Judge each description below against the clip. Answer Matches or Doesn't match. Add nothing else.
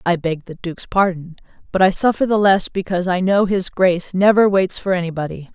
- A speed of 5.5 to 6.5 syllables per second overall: Matches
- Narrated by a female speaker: Matches